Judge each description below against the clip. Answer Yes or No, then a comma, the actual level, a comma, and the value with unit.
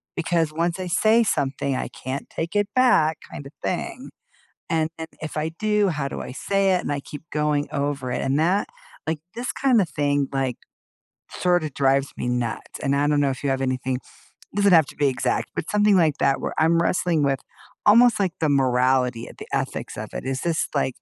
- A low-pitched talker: No, medium, 150 Hz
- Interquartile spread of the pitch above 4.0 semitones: Yes, average, 4.6 semitones